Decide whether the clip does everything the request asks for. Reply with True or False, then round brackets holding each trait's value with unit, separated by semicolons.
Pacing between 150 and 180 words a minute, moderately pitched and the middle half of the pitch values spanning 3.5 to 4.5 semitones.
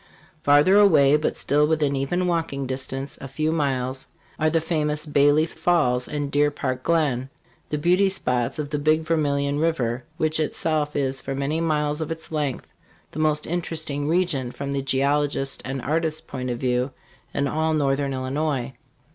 False (165 wpm; 145 Hz; 2.5 semitones)